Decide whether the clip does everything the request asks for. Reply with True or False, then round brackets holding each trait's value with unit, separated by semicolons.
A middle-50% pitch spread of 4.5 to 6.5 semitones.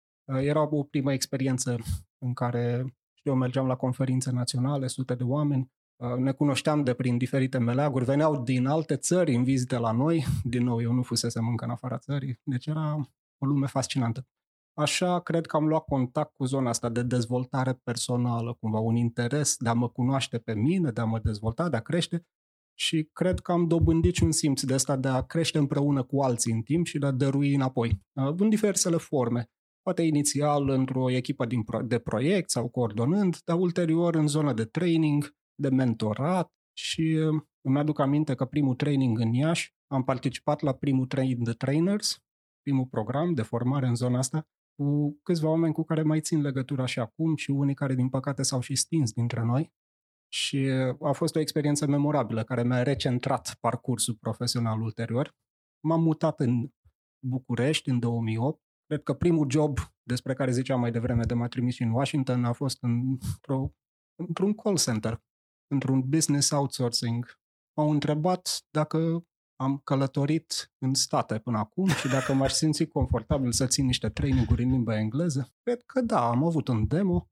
False (3.7 semitones)